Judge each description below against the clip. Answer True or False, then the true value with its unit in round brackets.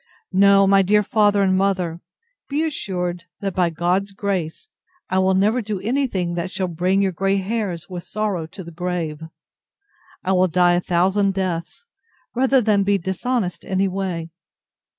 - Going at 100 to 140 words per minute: False (165 wpm)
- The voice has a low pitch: False (190 Hz)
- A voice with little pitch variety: True (2.3 semitones)